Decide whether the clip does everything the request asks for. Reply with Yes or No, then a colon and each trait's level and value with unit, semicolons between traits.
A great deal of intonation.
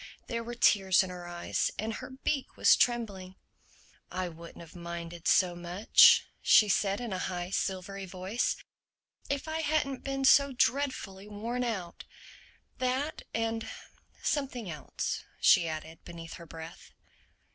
Yes: wide, 6.0 semitones